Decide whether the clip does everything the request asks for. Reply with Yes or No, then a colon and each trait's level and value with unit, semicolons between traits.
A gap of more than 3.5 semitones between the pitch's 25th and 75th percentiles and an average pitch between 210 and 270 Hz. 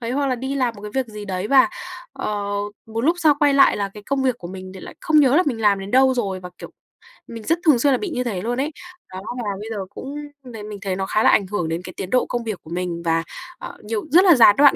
Yes: average, 5.2 semitones; high, 225 Hz